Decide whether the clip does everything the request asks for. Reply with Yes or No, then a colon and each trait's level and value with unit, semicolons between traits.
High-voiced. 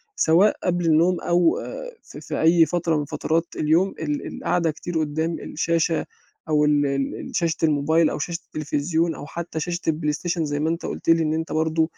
No: medium, 160 Hz